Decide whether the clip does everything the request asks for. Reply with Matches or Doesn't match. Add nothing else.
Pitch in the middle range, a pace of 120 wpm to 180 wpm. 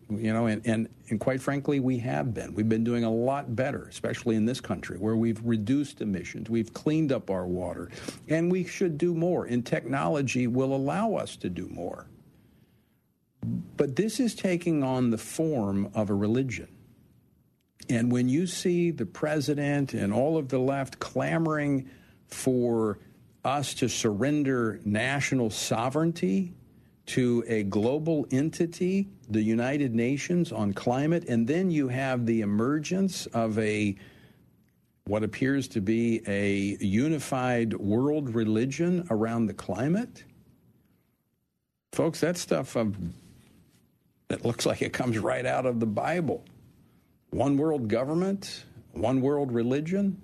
Doesn't match